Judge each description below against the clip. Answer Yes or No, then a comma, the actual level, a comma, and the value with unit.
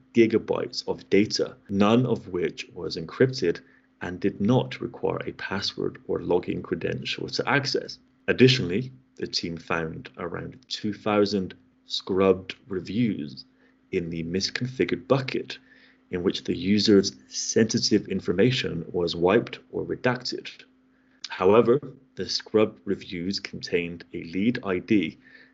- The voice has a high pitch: No, low, 100 Hz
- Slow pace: Yes, slow, 115 wpm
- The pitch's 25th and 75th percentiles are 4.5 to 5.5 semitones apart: Yes, average, 5.2 semitones